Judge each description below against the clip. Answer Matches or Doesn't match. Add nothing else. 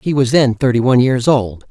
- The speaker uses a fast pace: Matches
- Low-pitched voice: Matches